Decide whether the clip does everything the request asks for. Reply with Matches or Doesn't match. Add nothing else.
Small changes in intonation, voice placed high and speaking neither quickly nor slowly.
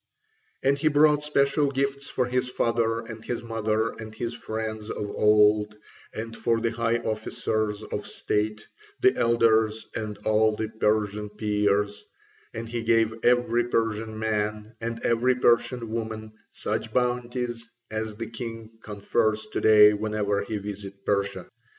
Doesn't match